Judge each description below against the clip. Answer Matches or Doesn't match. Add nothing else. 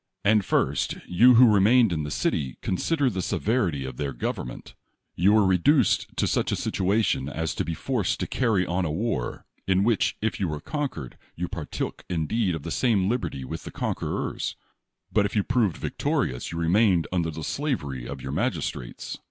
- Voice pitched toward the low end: Matches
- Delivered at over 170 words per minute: Matches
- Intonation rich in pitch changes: Matches